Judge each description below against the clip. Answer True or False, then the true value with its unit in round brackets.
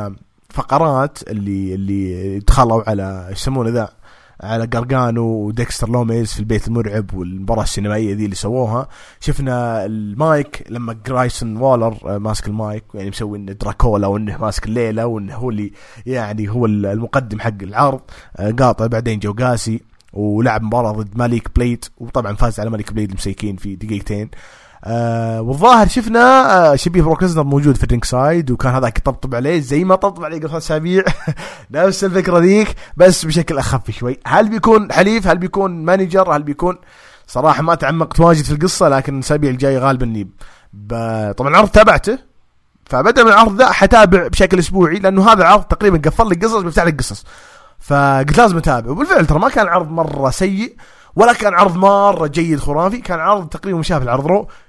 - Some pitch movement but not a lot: False (7.6 semitones)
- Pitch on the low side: True (130 Hz)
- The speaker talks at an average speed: True (160 wpm)